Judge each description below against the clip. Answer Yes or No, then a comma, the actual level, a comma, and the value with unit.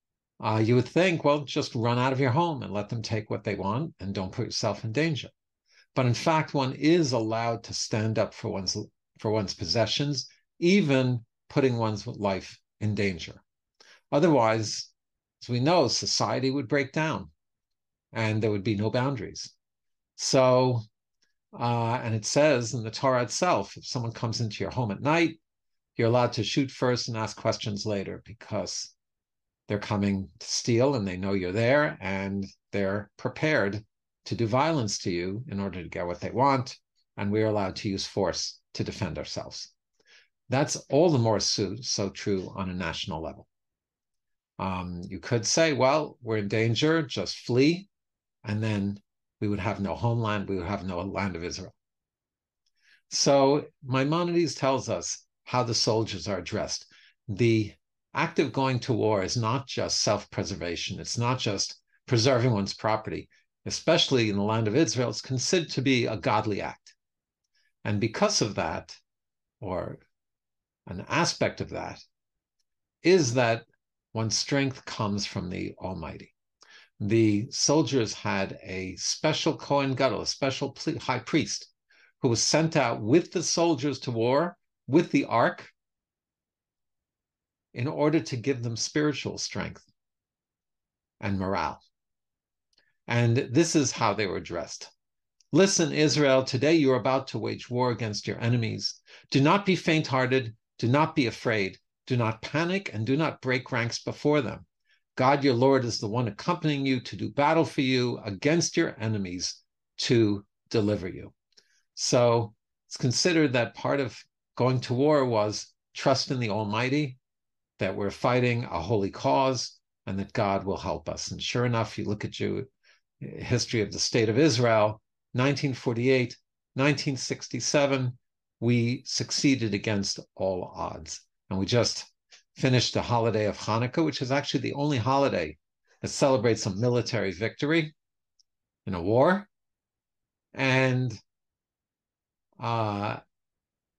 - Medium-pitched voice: No, low, 115 Hz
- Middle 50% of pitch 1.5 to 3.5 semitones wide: No, average, 4.7 semitones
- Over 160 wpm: No, average, 155 wpm